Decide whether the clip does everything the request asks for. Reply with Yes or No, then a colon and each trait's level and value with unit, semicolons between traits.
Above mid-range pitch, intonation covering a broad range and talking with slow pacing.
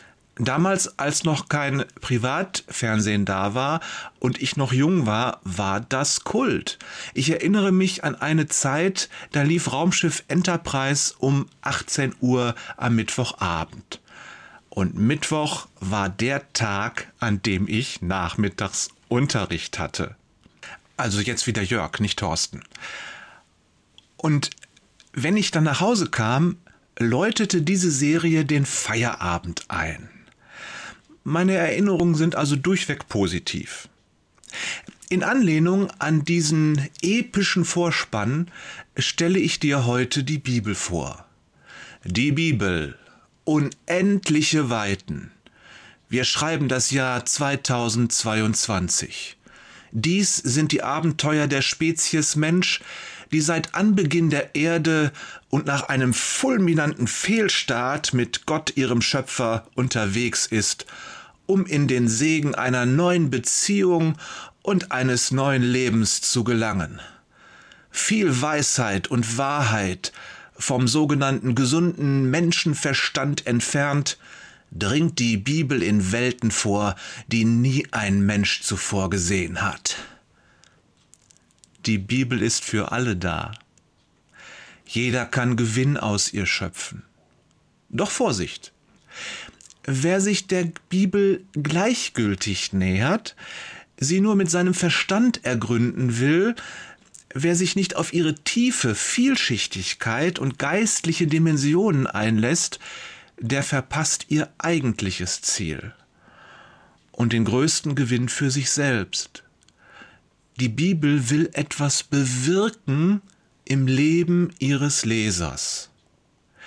No: medium, 140 Hz; wide, 6.3 semitones; slow, 105 wpm